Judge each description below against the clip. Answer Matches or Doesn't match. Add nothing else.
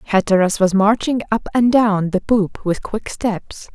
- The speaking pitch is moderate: Doesn't match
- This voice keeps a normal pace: Matches